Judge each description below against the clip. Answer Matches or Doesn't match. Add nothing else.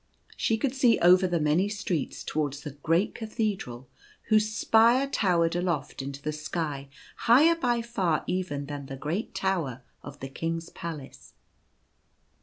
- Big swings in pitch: Matches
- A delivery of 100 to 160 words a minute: Matches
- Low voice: Doesn't match